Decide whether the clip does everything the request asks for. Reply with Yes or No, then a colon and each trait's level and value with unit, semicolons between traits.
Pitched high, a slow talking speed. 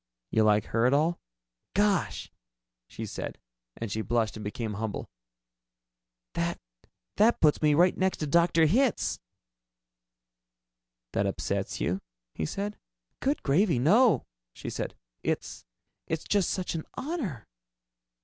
No: medium, 155 Hz; slow, 130 wpm